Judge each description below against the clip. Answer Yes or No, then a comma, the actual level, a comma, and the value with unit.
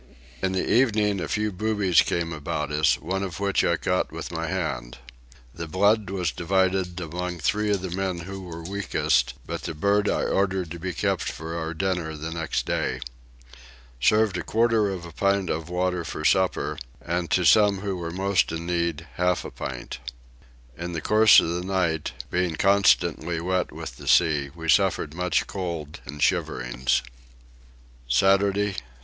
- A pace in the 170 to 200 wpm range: Yes, average, 175 wpm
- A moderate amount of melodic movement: Yes, average, 3.0 semitones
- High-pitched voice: No, very low, 90 Hz